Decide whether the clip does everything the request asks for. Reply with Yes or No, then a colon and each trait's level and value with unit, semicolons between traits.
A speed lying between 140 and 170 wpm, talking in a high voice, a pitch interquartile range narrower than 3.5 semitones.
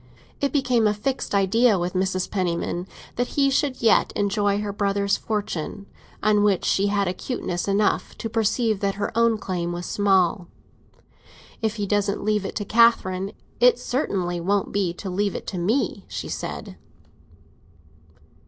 Yes: average, 155 wpm; high, 205 Hz; average, 2.8 semitones